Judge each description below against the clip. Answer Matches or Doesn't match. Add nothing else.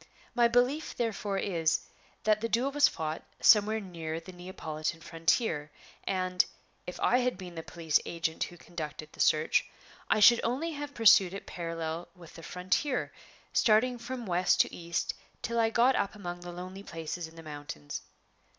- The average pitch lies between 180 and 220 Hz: Matches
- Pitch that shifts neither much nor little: Doesn't match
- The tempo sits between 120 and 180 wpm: Matches